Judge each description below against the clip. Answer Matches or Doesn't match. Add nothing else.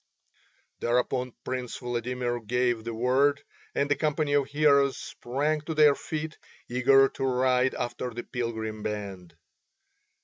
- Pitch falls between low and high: Doesn't match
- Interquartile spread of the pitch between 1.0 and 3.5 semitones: Matches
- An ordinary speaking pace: Doesn't match